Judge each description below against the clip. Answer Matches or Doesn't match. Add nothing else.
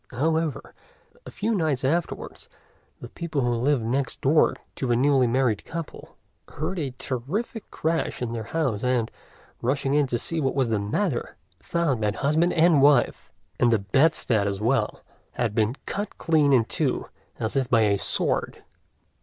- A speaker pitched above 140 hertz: Doesn't match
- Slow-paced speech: Doesn't match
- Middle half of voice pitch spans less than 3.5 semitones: Doesn't match